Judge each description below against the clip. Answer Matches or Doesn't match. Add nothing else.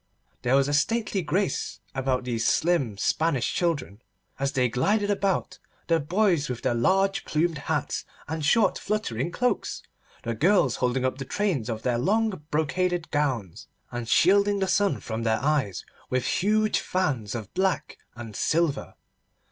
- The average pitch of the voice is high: Doesn't match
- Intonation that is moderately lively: Doesn't match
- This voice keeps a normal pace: Matches